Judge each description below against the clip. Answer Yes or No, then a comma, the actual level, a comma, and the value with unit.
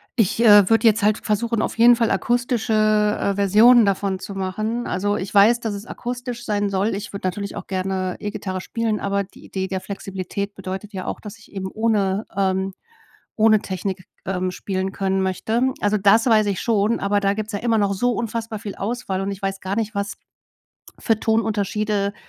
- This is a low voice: No, high, 205 Hz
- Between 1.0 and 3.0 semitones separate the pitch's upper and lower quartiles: Yes, narrow, 2.5 semitones